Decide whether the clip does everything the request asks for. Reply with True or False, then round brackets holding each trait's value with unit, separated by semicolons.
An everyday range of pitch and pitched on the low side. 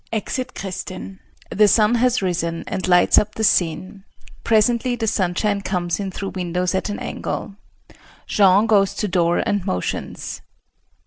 False (3.0 semitones; 195 Hz)